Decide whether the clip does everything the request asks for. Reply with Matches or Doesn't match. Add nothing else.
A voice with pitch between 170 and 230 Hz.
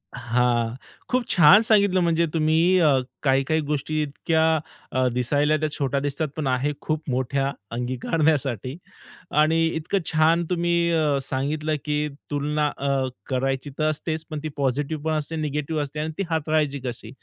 Doesn't match